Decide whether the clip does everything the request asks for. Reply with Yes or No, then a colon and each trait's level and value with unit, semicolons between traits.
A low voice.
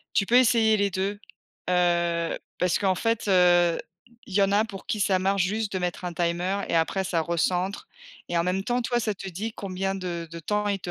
No: high, 190 Hz